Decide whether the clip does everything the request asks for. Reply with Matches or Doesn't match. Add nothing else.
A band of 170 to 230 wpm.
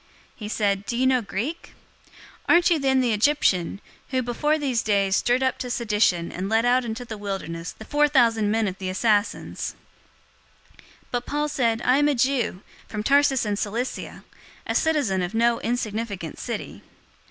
Matches